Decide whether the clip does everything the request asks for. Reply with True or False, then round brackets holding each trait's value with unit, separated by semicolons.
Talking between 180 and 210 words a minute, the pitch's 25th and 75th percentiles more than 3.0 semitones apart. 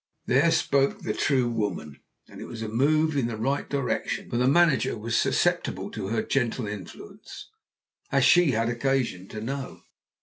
False (170 wpm; 3.6 semitones)